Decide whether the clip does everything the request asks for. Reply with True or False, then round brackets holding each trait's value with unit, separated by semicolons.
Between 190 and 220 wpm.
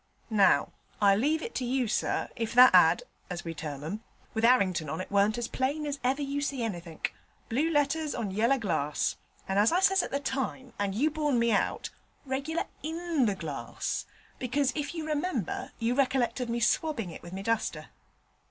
True (195 wpm)